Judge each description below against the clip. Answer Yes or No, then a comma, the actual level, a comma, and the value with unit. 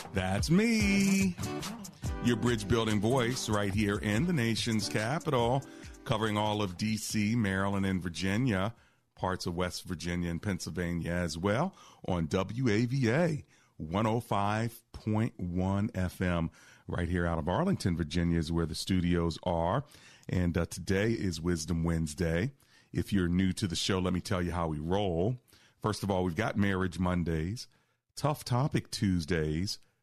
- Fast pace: No, average, 140 wpm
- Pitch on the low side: Yes, low, 100 Hz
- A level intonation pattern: No, average, 4.8 semitones